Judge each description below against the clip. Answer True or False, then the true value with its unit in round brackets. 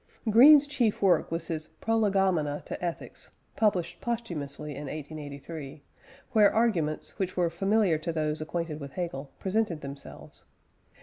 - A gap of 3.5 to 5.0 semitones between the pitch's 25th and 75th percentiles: False (5.4 semitones)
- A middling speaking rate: False (130 wpm)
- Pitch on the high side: False (170 Hz)